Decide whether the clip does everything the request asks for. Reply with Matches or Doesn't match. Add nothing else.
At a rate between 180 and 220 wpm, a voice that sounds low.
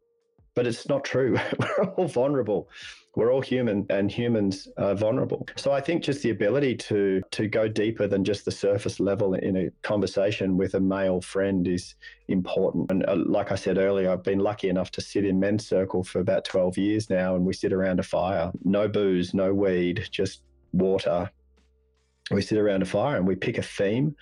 Matches